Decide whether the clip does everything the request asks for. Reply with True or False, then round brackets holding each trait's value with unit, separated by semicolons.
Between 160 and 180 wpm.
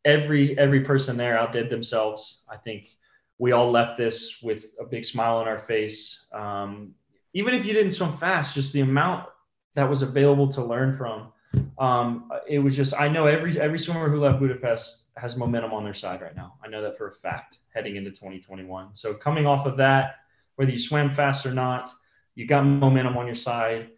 False (200 wpm)